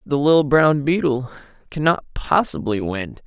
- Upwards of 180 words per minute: No, average, 145 wpm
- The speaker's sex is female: No, male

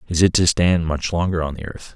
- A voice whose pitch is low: Yes, very low, 85 Hz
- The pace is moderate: No, fast, 275 wpm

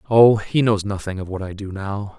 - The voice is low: Yes, low, 100 Hz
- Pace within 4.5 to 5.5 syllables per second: Yes, 5.0 syllables/s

